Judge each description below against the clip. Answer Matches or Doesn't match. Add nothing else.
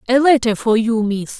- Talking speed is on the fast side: Matches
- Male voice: Doesn't match